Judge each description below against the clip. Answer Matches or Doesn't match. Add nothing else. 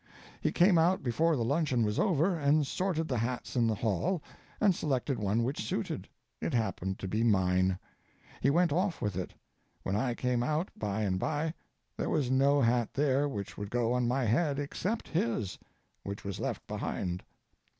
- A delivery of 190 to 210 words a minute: Doesn't match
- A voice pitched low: Matches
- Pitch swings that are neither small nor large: Doesn't match